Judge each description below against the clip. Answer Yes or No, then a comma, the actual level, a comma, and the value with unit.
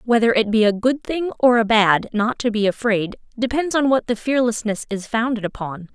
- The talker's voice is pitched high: Yes, high, 230 Hz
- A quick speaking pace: Yes, fast, 210 wpm